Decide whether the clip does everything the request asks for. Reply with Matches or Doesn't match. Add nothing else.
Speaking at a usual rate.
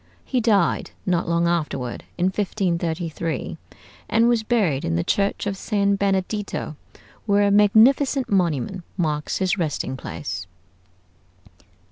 Doesn't match